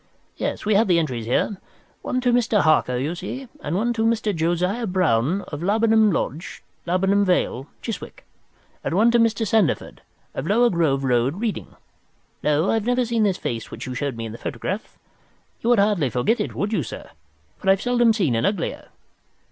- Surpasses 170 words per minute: Yes, average, 190 wpm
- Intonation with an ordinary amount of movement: No, wide, 6.9 semitones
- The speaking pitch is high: Yes, high, 195 Hz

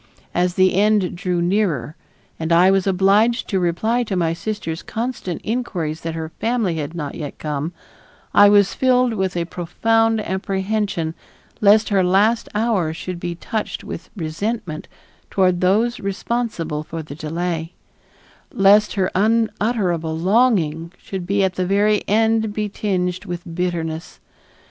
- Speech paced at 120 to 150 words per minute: Yes, average, 140 wpm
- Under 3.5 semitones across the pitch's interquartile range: No, average, 4.0 semitones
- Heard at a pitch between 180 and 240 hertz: Yes, high, 190 Hz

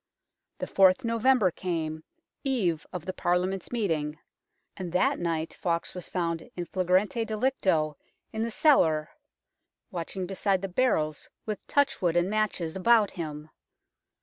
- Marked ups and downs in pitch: No, average, 4.4 semitones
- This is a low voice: No, medium, 185 Hz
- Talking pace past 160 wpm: No, slow, 135 wpm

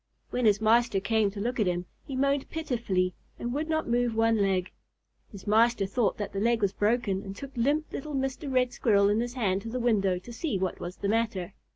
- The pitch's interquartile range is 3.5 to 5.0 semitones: Yes, average, 3.8 semitones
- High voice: Yes, high, 225 Hz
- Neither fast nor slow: No, fast, 225 wpm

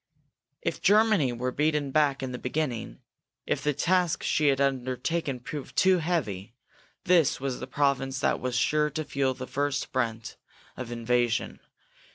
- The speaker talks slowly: No, average, 155 wpm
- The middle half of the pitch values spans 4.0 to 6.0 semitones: No, average, 3.3 semitones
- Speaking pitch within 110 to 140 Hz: Yes, low, 135 Hz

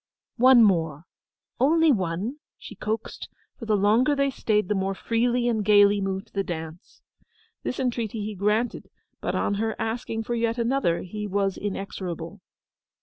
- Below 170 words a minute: Yes, average, 145 wpm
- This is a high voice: Yes, high, 210 Hz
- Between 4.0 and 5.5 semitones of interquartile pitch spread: No, average, 3.4 semitones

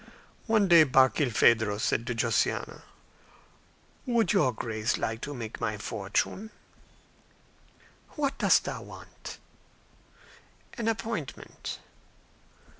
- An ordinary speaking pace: No, slow, 95 wpm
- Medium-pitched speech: No, low, 130 Hz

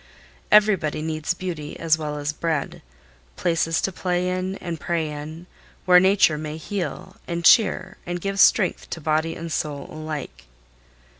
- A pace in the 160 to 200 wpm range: No, average, 150 wpm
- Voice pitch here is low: No, medium, 165 Hz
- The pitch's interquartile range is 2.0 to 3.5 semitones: Yes, average, 3.0 semitones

